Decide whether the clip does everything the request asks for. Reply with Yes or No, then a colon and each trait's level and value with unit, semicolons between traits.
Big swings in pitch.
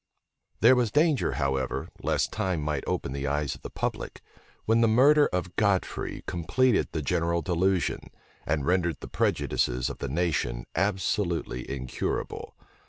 Yes: wide, 6.5 semitones